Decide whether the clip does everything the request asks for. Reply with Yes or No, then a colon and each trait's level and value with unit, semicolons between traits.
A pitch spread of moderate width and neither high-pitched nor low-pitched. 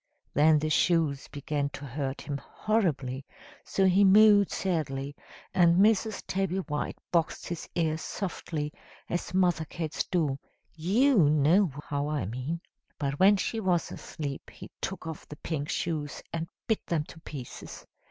Yes: average, 4.4 semitones; medium, 160 Hz